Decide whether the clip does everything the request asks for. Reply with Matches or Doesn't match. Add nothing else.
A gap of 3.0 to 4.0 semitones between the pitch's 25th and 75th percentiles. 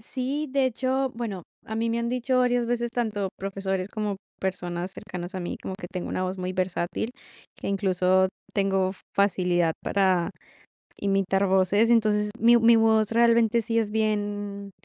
Matches